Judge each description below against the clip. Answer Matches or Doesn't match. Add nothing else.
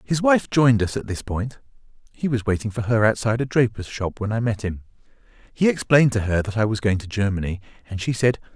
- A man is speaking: Matches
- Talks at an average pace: Doesn't match